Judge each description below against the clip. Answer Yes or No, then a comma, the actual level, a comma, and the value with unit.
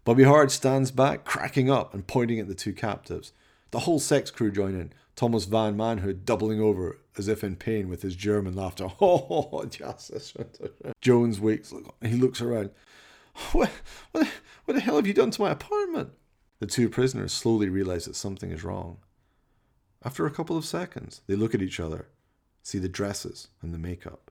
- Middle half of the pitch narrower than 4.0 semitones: No, average, 4.3 semitones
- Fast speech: No, average, 180 wpm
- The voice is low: Yes, low, 105 Hz